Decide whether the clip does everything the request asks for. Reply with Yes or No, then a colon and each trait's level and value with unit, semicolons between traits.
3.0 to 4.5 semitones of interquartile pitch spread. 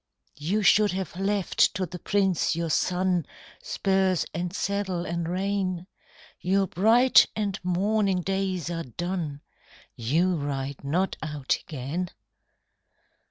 No: narrow, 2.6 semitones